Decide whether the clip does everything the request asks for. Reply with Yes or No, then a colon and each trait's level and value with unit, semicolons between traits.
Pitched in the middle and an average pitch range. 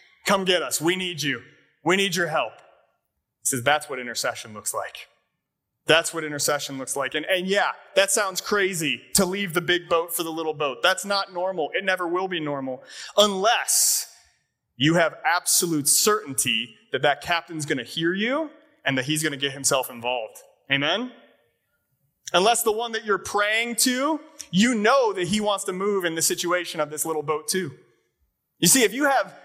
Yes: medium, 175 Hz; average, 4.9 semitones